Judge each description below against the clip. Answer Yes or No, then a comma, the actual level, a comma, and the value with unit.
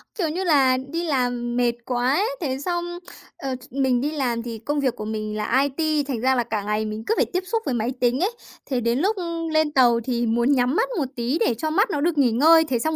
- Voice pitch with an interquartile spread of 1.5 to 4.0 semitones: No, average, 4.7 semitones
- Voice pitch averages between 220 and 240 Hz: No, very high, 265 Hz